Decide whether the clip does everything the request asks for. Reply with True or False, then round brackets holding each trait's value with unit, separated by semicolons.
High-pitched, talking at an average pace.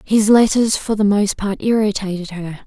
True (205 Hz; 180 wpm)